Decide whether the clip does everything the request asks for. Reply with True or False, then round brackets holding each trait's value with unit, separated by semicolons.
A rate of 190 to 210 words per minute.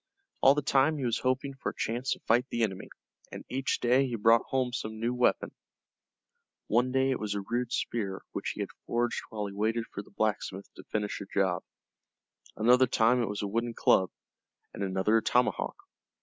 True (200 wpm)